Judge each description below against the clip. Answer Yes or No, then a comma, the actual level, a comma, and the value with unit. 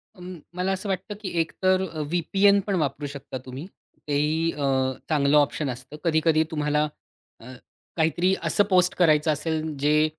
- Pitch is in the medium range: Yes, medium, 160 Hz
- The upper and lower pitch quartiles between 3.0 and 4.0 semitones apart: Yes, average, 3.6 semitones